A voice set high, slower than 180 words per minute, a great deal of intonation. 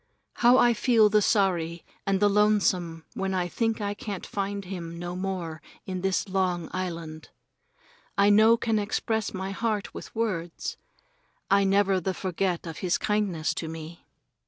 No: high, 195 Hz; average, 160 wpm; average, 3.0 semitones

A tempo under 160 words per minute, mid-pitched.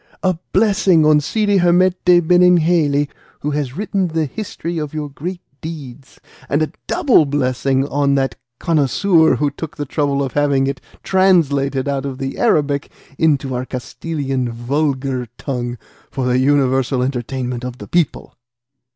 Yes: average, 145 wpm; medium, 145 Hz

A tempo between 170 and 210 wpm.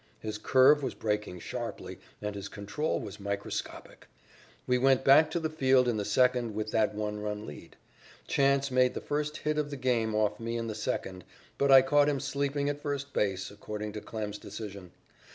Yes: average, 190 wpm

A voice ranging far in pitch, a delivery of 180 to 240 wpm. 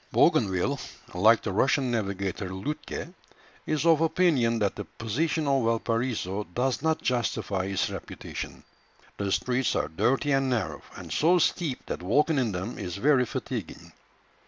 No: wide, 6.1 semitones; average, 145 wpm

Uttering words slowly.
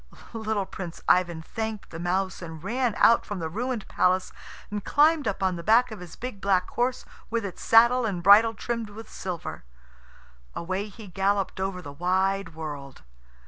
No: average, 175 wpm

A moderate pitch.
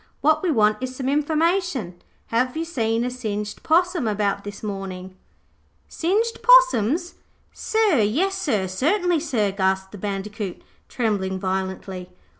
No: high, 230 Hz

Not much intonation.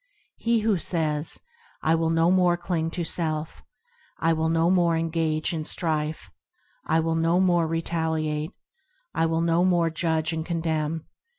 Yes: narrow, 1.2 semitones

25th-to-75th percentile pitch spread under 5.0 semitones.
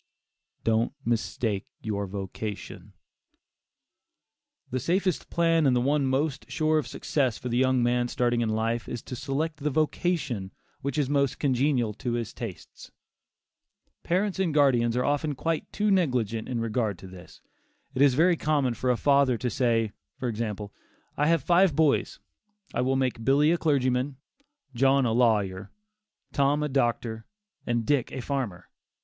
Yes: average, 4.1 semitones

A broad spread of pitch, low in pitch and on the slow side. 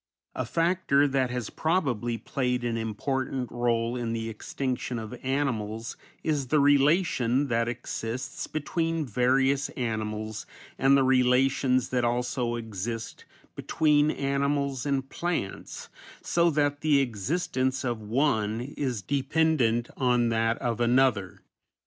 No: average, 3.3 semitones; low, 125 Hz; slow, 120 wpm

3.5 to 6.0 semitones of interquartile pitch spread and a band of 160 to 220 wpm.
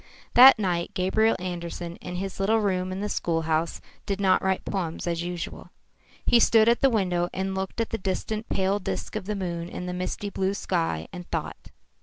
No: average, 2.7 semitones; average, 195 wpm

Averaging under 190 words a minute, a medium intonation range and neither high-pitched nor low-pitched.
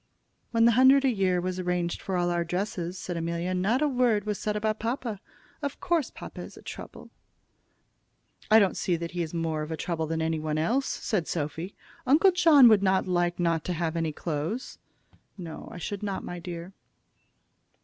No: average, 195 wpm; average, 4.6 semitones; medium, 180 Hz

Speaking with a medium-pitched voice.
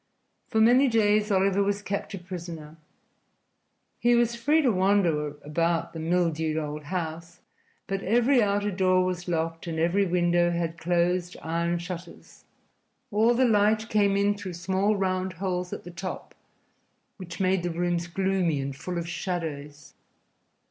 Yes: medium, 180 Hz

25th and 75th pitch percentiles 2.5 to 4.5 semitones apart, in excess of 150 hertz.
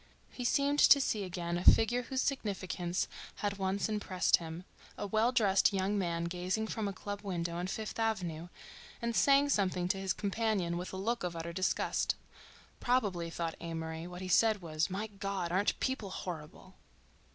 Yes: average, 3.9 semitones; high, 190 Hz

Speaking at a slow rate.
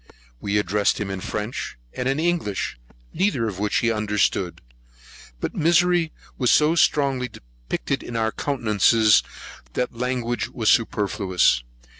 Yes: slow, 130 wpm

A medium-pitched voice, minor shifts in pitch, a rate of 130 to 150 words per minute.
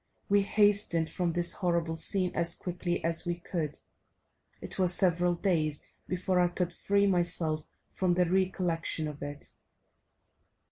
Yes: medium, 175 Hz; narrow, 1.9 semitones; average, 140 wpm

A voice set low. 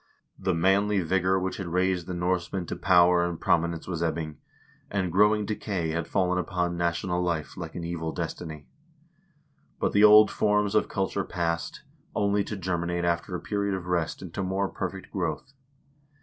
Yes: very low, 90 Hz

